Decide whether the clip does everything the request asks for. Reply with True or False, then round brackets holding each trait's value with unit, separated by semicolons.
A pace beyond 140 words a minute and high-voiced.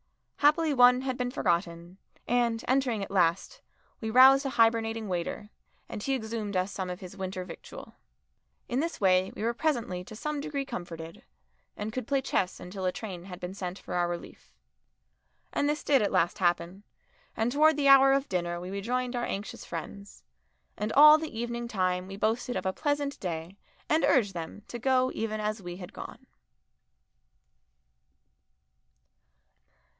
True (170 wpm; 215 Hz)